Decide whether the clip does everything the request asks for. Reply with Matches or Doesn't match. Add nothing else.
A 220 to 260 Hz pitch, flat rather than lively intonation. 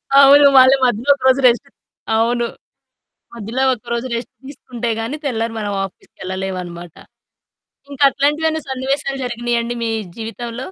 Doesn't match